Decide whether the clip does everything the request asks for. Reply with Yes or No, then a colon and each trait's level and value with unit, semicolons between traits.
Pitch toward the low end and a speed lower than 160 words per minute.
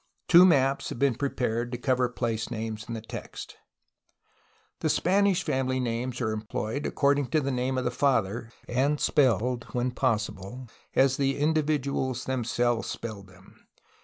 Yes: low, 125 Hz; average, 145 wpm